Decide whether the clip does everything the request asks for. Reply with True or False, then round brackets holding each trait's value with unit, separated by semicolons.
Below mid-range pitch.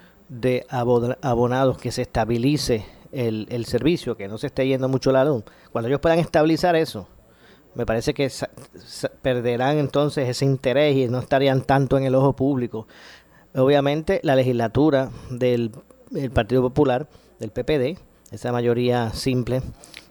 True (130 Hz)